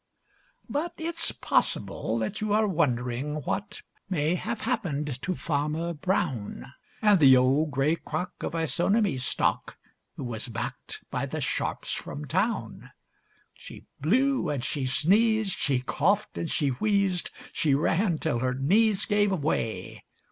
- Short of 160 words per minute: Yes, average, 140 wpm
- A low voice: No, medium, 160 Hz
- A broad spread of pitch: Yes, wide, 7.0 semitones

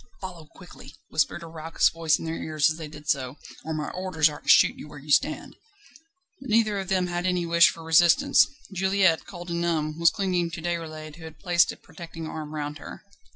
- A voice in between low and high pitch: Yes, medium, 165 Hz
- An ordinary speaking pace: No, fast, 215 wpm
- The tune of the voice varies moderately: No, narrow, 2.3 semitones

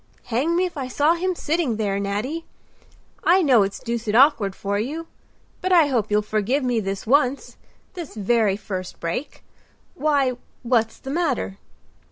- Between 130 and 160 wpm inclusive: Yes, average, 155 wpm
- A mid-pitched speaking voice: No, high, 245 Hz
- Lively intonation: Yes, wide, 6.4 semitones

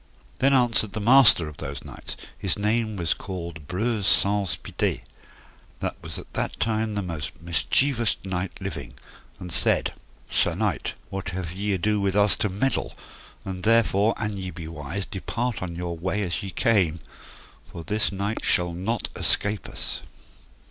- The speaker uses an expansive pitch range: No, average, 3.7 semitones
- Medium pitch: No, very low, 95 Hz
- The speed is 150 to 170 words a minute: Yes, average, 165 wpm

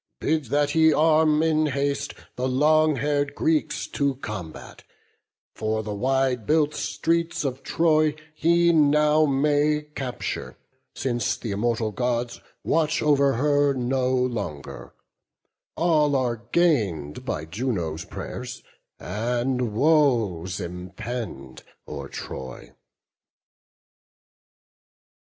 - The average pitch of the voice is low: Yes, low, 130 Hz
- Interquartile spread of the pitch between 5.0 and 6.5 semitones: Yes, wide, 5.6 semitones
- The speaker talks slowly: Yes, slow, 100 wpm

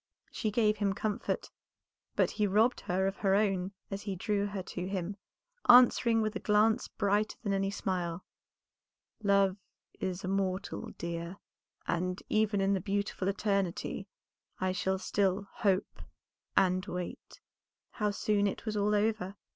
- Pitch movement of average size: No, narrow, 1.9 semitones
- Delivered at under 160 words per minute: Yes, average, 145 wpm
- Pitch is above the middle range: Yes, high, 200 Hz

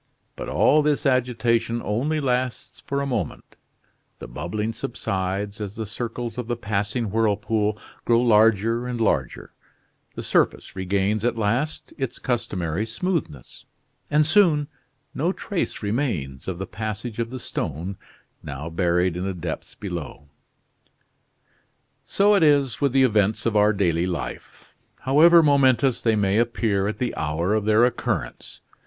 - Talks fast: No, average, 145 wpm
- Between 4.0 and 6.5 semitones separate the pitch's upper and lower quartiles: Yes, average, 4.4 semitones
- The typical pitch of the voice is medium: No, low, 110 Hz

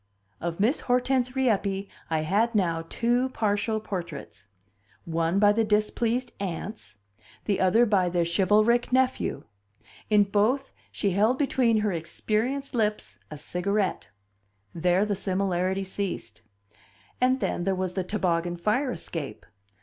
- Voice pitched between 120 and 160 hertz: No, high, 205 Hz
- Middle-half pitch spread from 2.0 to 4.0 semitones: No, average, 4.5 semitones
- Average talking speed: No, slow, 130 wpm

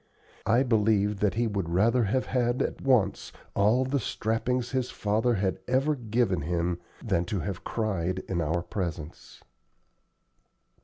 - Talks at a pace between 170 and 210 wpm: No, average, 145 wpm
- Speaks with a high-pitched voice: No, low, 105 Hz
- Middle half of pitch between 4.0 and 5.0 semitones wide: Yes, average, 4.6 semitones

